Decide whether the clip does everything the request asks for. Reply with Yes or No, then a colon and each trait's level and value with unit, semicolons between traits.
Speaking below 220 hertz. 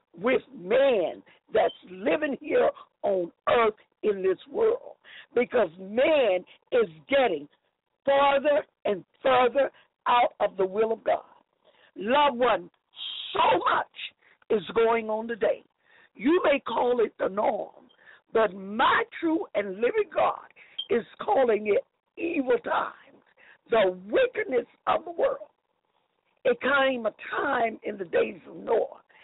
No: very high, 290 Hz